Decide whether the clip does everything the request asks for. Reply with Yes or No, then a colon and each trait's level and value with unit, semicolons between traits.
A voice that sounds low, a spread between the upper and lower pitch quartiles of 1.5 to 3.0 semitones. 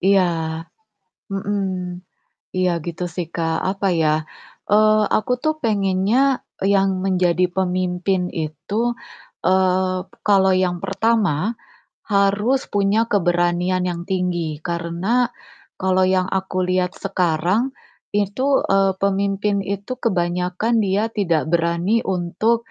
No: high, 190 Hz; narrow, 2.5 semitones